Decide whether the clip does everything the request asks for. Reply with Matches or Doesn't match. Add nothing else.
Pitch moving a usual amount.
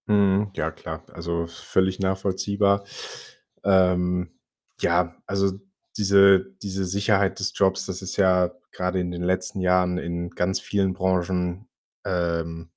Doesn't match